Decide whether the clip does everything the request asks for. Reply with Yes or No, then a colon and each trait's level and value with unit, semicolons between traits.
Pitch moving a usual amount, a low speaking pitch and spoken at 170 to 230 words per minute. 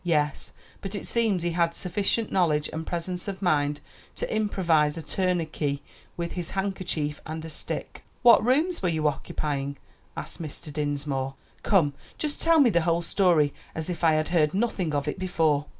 No: average, 4.0 semitones; medium, 170 Hz; average, 175 wpm